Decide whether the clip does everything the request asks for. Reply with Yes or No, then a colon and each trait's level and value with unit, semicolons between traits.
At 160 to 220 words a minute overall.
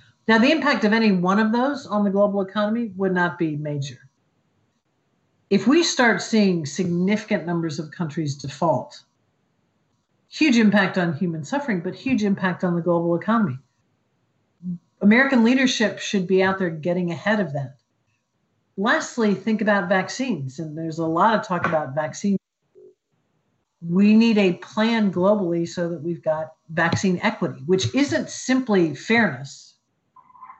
No: average, 145 wpm